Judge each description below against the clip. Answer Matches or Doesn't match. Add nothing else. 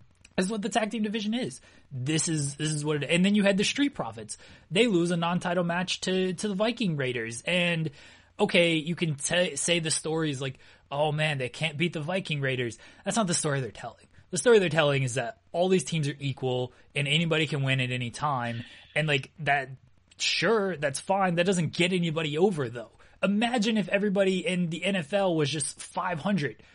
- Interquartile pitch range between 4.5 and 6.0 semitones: Matches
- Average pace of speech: Doesn't match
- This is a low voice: Doesn't match